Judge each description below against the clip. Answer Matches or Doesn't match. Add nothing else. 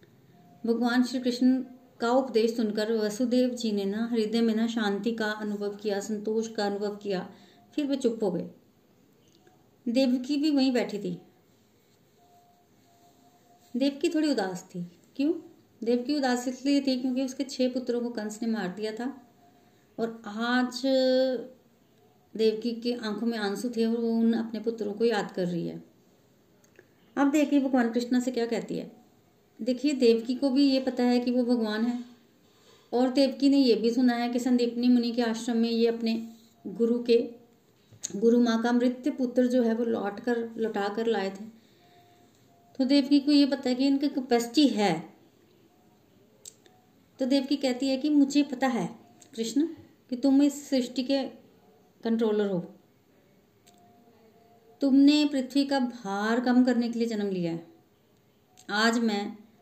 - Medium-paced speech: Matches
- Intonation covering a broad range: Doesn't match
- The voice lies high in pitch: Matches